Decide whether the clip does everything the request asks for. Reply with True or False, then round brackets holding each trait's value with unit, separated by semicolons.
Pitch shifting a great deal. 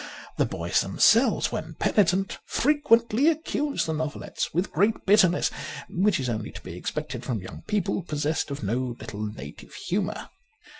True (9.0 semitones)